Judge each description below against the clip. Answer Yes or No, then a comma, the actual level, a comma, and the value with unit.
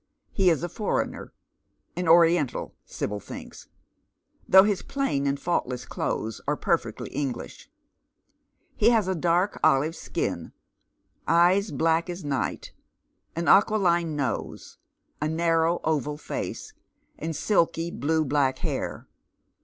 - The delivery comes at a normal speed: No, slow, 130 wpm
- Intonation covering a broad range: No, average, 3.4 semitones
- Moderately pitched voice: Yes, medium, 165 Hz